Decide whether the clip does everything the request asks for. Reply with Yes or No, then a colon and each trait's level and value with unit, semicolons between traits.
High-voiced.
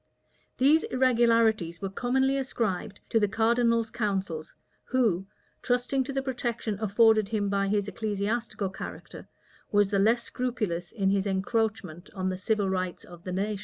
Yes: high, 215 Hz